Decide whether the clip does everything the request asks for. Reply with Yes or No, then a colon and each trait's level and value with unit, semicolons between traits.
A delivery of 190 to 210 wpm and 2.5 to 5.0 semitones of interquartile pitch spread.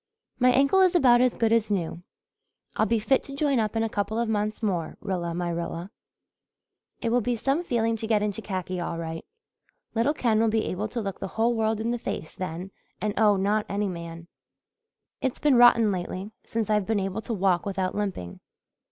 Yes: fast, 205 wpm; average, 3.7 semitones